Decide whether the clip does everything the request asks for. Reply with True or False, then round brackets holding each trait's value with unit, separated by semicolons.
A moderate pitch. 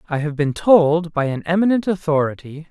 True (165 Hz)